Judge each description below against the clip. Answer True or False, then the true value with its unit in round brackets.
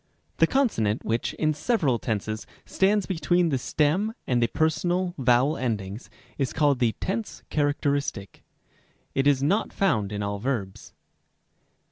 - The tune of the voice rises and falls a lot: True (7.3 semitones)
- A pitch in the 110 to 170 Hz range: True (140 Hz)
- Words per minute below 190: True (140 wpm)